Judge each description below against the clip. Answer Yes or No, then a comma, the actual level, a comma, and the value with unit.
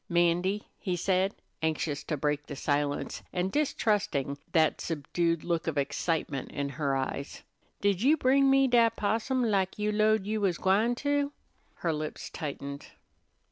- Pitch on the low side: No, medium, 180 Hz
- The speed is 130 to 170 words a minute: Yes, average, 150 wpm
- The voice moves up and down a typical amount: No, wide, 6.4 semitones